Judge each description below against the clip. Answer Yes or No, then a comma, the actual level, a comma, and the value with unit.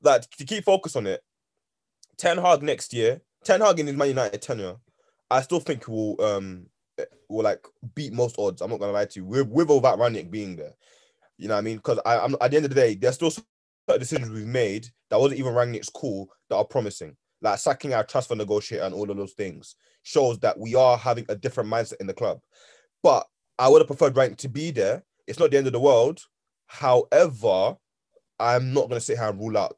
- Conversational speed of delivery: No, fast, 230 wpm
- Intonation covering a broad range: Yes, wide, 6.1 semitones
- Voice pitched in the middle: No, low, 125 Hz